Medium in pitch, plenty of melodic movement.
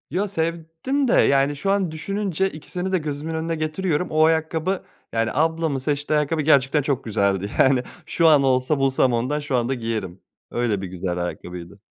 No: medium, 150 Hz; average, 4.6 semitones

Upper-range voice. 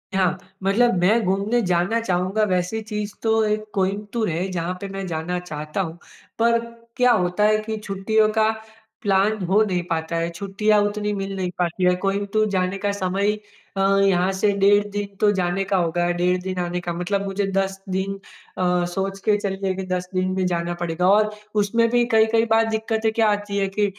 Yes: high, 195 Hz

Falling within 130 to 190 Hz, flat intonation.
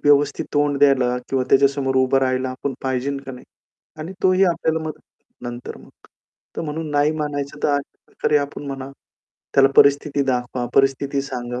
Yes: medium, 140 Hz; narrow, 1.9 semitones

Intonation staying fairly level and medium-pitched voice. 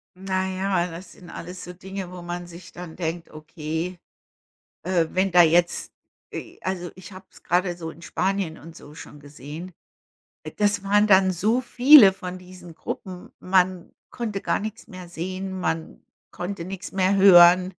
Yes: narrow, 1.8 semitones; medium, 180 Hz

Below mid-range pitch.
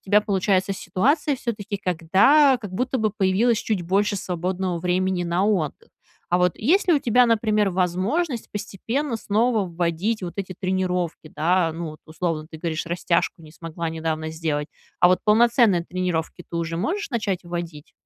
No: medium, 185 Hz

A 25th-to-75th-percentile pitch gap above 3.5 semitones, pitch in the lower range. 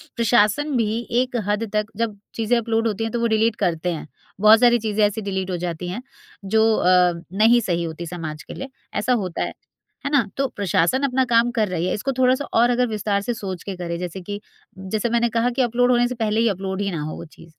No: average, 4.3 semitones; high, 215 Hz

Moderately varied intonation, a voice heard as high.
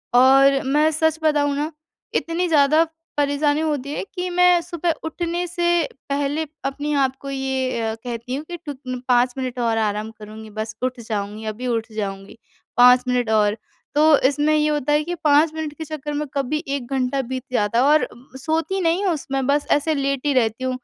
Yes: average, 3.8 semitones; very high, 275 Hz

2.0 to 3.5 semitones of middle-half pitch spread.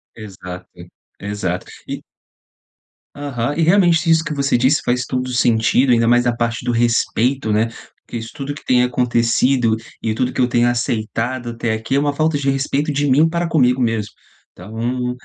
Yes: average, 3.2 semitones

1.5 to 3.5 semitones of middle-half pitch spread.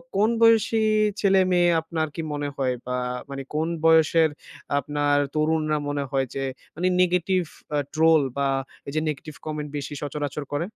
Yes: average, 3.1 semitones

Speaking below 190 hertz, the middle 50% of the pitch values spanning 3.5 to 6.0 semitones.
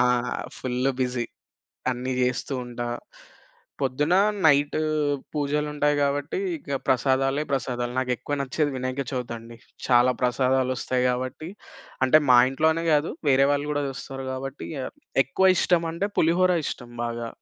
No: low, 135 Hz; average, 2.7 semitones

